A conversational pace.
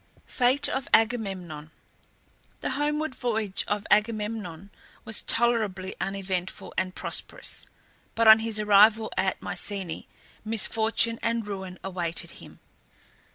No: slow, 110 wpm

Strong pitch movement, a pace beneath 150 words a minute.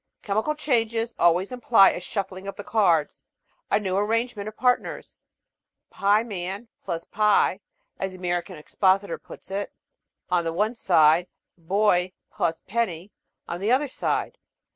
No: average, 3.9 semitones; average, 140 wpm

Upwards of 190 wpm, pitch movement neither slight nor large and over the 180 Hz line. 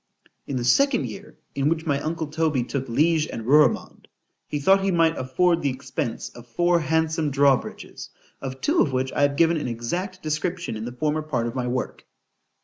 No: average, 200 wpm; average, 4.3 semitones; medium, 150 Hz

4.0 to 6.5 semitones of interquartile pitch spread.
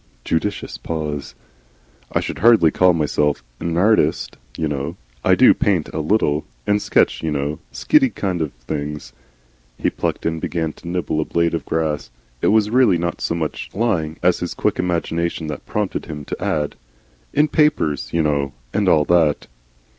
No: average, 3.5 semitones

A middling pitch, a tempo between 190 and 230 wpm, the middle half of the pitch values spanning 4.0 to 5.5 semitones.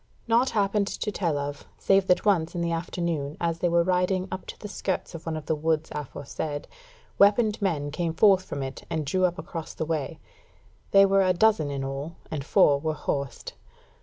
Yes: medium, 170 Hz; average, 200 wpm; average, 4.4 semitones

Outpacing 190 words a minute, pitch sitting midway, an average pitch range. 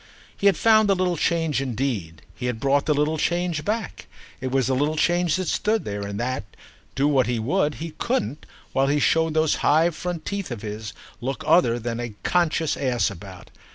No: average, 200 wpm; medium, 145 Hz; wide, 6.1 semitones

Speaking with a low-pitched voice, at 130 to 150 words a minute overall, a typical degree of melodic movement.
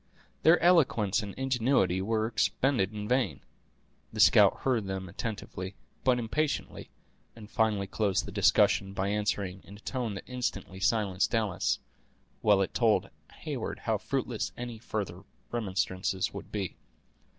Yes: low, 105 Hz; average, 140 wpm; average, 3.8 semitones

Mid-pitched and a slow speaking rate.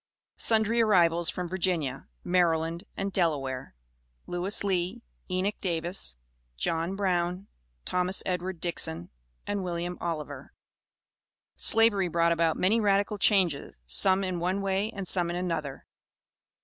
Yes: medium, 180 Hz; slow, 120 wpm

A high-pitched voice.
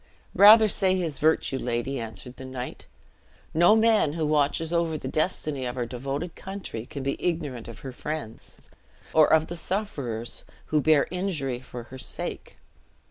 No: medium, 150 Hz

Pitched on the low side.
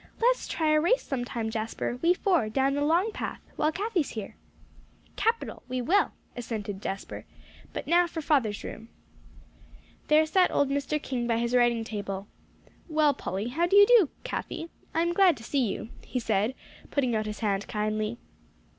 No: very high, 265 Hz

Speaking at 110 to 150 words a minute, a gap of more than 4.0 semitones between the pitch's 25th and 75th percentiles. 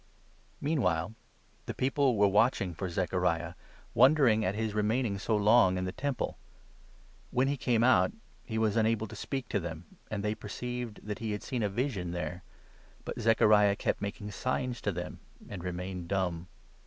No: average, 180 wpm; average, 4.5 semitones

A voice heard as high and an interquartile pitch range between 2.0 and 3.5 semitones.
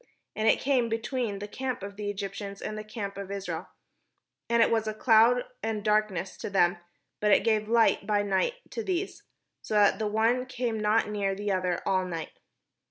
Yes: high, 210 Hz; narrow, 2.4 semitones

